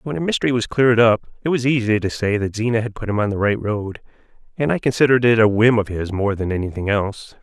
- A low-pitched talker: Yes, low, 110 Hz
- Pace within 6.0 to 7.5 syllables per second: Yes, 6.5 syllables/s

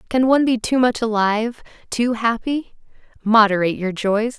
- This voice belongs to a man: No, female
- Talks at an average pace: Yes, average, 150 wpm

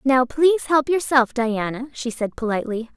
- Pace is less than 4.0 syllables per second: No, 5.1 syllables/s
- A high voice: Yes, very high, 255 Hz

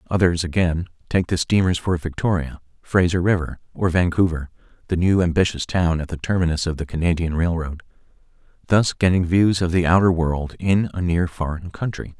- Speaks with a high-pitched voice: No, very low, 85 Hz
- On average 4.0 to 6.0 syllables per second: Yes, 5.3 syllables/s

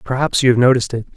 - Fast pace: Yes, fast, 260 wpm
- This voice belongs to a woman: No, male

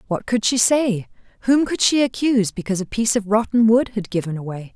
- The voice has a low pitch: No, high, 220 Hz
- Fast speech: Yes, fast, 215 wpm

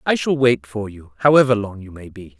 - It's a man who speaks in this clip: Yes, male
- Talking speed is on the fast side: Yes, fast, 250 wpm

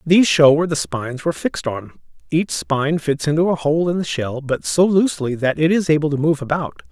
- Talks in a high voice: No, medium, 150 Hz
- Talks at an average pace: No, fast, 235 wpm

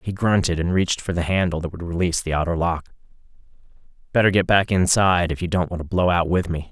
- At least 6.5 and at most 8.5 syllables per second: Yes, 6.6 syllables/s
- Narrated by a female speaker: No, male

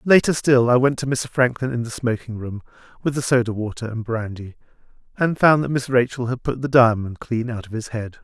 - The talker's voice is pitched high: No, low, 120 Hz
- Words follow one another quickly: Yes, fast, 225 wpm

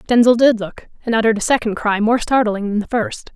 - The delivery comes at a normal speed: No, fast, 230 wpm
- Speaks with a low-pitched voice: No, high, 225 Hz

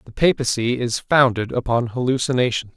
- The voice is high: No, low, 125 Hz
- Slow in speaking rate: Yes, slow, 130 wpm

